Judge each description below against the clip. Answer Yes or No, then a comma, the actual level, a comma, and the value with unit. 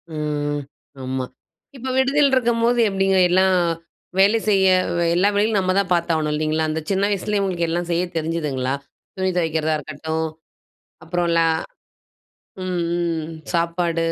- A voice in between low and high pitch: Yes, medium, 175 Hz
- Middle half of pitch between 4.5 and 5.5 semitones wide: No, average, 3.6 semitones